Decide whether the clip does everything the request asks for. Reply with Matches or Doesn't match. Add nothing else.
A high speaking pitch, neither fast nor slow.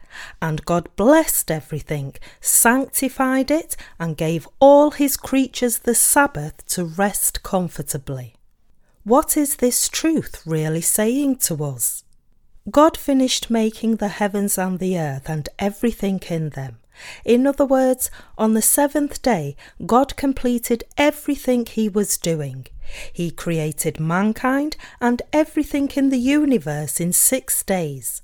Doesn't match